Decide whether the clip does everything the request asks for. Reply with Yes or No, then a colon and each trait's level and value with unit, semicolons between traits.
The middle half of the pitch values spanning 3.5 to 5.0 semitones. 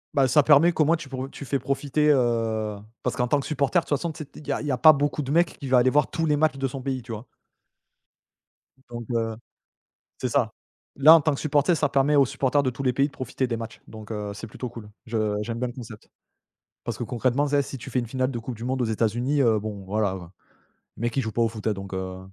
Yes: average, 4.0 semitones